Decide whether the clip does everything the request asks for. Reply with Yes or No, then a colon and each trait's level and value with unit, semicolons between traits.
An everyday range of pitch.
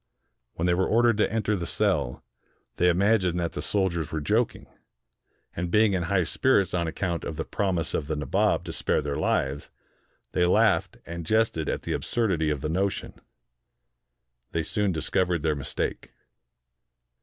Yes: average, 3.7 semitones